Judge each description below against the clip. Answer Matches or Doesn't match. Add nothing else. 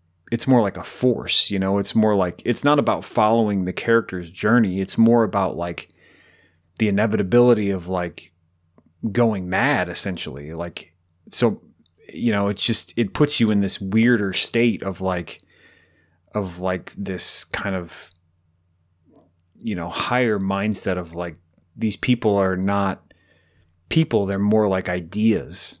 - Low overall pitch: Matches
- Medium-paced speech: Matches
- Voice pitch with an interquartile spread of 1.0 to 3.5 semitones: Doesn't match